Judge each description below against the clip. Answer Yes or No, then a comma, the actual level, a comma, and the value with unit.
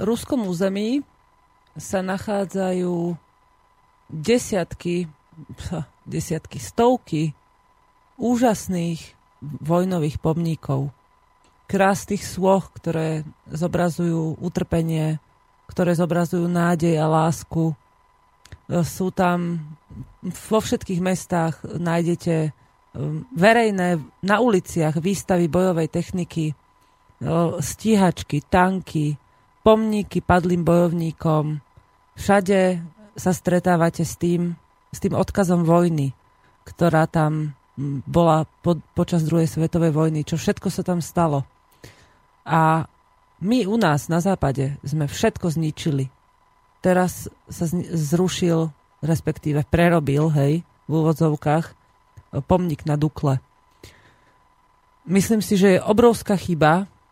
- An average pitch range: Yes, average, 3.1 semitones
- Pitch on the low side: No, medium, 170 Hz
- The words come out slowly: Yes, slow, 90 wpm